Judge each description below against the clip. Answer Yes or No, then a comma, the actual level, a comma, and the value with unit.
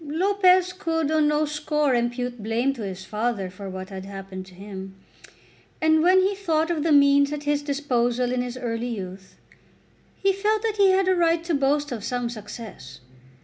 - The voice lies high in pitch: Yes, very high, 280 Hz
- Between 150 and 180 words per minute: No, average, 190 wpm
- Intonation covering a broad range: Yes, wide, 6.6 semitones